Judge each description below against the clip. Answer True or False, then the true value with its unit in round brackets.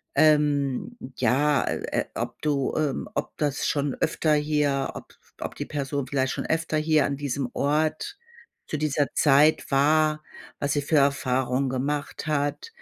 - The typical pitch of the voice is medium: True (145 Hz)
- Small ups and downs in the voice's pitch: True (1.8 semitones)